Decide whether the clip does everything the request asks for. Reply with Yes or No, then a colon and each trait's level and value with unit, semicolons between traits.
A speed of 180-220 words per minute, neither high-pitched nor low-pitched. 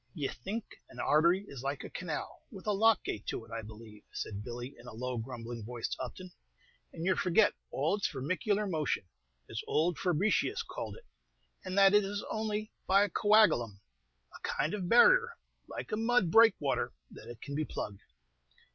Yes: average, 185 wpm; medium, 165 Hz